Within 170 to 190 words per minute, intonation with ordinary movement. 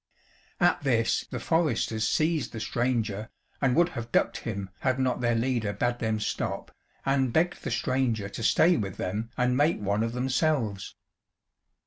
No: average, 160 wpm; average, 3.5 semitones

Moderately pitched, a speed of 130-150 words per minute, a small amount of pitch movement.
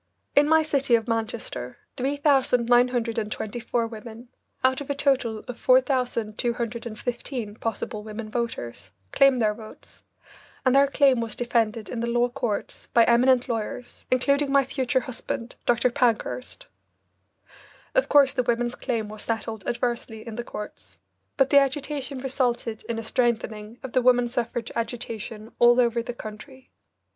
No: high, 240 Hz; average, 140 wpm; narrow, 2.3 semitones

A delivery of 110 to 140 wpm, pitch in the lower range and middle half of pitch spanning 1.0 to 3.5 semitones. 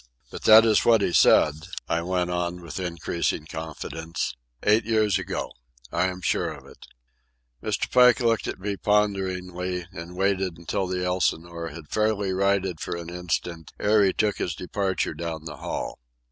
No: average, 165 wpm; very low, 90 Hz; average, 3.1 semitones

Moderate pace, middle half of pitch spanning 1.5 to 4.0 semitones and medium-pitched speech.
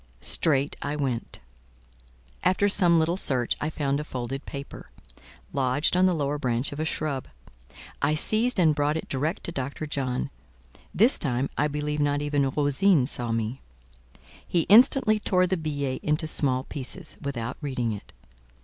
Yes: average, 160 wpm; average, 3.3 semitones; medium, 145 Hz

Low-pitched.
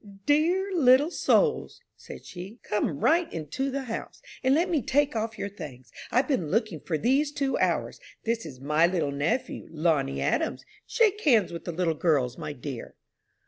No: high, 215 Hz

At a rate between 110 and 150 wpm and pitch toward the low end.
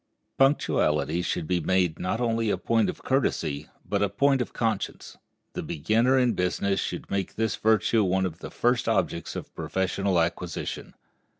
No: average, 165 wpm; low, 100 Hz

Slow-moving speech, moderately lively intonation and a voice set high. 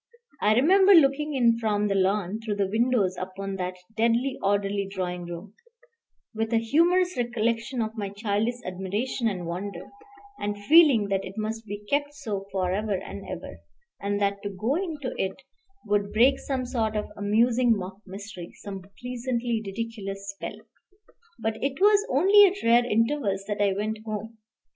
No: average, 160 wpm; average, 3.7 semitones; high, 215 Hz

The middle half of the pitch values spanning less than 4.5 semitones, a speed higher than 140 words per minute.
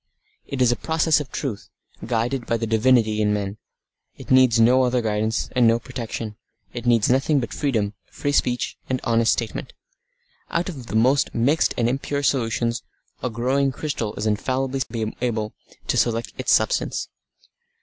Yes: average, 2.7 semitones; average, 160 wpm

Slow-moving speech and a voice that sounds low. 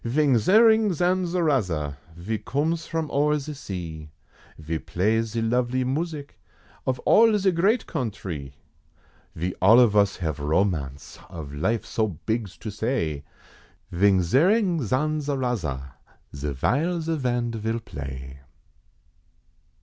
Yes: slow, 120 wpm; low, 115 Hz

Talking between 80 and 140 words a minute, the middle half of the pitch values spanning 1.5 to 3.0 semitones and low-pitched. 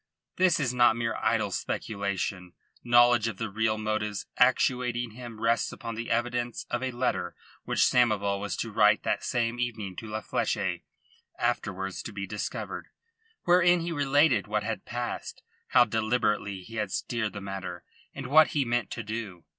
No: average, 165 wpm; average, 2.7 semitones; low, 115 Hz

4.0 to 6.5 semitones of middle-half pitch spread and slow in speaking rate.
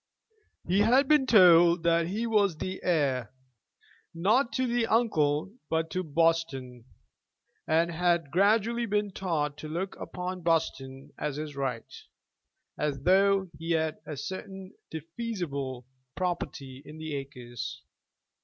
Yes: average, 4.9 semitones; slow, 125 wpm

